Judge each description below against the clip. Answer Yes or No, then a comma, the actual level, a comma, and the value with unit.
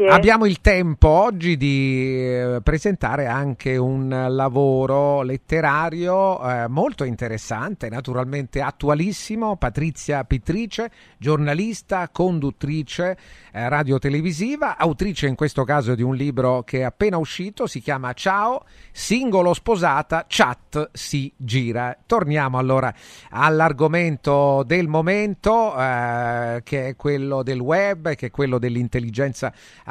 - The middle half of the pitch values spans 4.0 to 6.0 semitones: Yes, average, 5.1 semitones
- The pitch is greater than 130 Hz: Yes, medium, 140 Hz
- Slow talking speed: Yes, slow, 105 wpm